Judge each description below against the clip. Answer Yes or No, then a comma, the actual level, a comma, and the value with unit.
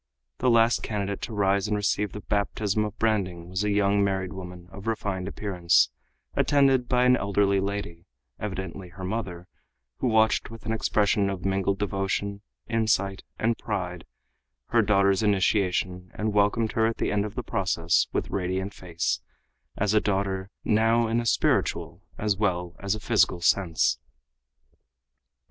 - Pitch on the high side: No, low, 100 Hz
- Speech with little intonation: Yes, narrow, 2.2 semitones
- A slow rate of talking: No, average, 155 wpm